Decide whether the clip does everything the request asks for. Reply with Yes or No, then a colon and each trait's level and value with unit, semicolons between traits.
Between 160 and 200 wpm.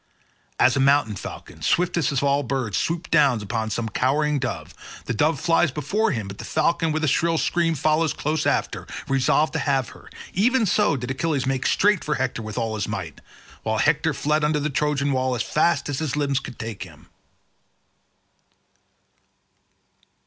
Yes: average, 170 wpm